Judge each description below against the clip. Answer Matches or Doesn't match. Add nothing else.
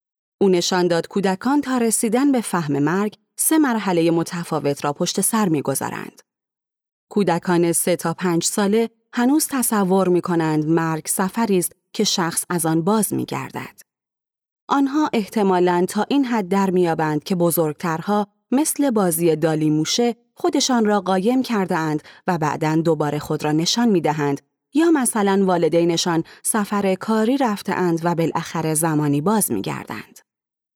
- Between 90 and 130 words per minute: Doesn't match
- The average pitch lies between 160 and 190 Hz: Matches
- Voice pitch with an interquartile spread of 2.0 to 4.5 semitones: Doesn't match